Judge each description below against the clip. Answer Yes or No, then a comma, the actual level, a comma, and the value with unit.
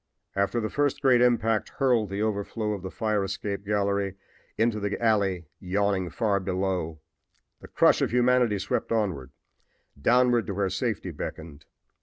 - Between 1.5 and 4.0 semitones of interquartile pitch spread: Yes, average, 3.1 semitones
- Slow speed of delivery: No, average, 155 wpm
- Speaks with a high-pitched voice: No, low, 100 Hz